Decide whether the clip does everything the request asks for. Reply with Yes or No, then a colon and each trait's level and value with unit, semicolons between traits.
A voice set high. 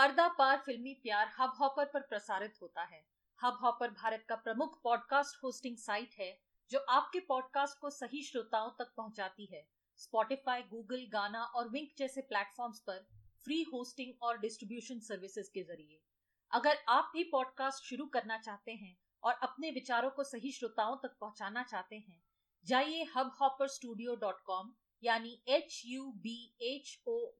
Yes: high, 245 Hz